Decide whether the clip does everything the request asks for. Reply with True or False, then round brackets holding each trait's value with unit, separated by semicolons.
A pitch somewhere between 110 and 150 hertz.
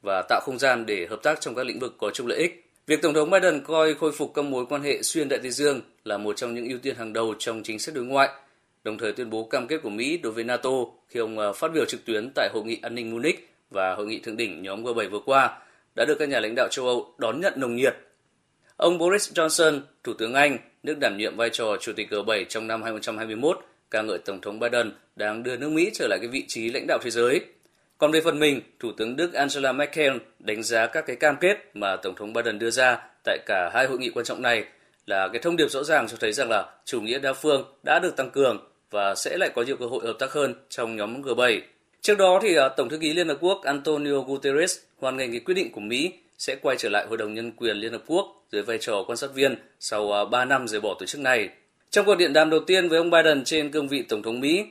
True (140 Hz)